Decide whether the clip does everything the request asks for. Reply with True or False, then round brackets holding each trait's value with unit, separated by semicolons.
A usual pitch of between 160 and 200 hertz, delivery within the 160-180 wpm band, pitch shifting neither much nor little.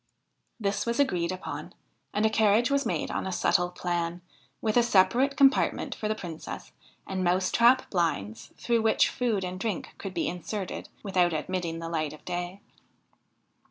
True (190 Hz; 165 wpm; 4.1 semitones)